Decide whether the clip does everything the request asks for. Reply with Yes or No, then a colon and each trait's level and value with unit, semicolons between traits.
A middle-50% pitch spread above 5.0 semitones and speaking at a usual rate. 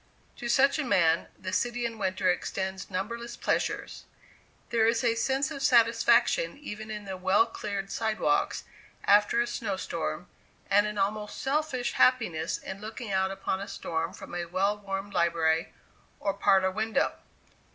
No: average, 3.7 semitones; average, 155 wpm